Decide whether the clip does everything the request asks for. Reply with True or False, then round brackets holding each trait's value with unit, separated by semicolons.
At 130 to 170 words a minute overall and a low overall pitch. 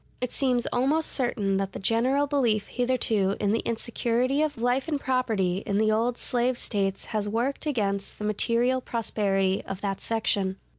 False (165 wpm; 230 Hz)